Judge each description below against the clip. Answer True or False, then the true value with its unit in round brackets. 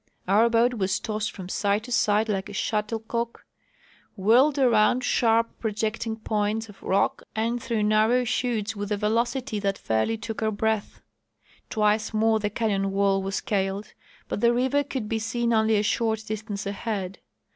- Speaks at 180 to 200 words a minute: False (165 wpm)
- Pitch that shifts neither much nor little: False (2.0 semitones)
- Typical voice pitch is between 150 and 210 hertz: False (220 Hz)